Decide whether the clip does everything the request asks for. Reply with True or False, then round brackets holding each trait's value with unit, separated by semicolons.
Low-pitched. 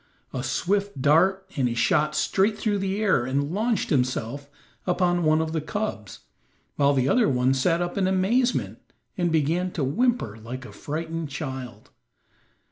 False (160 Hz)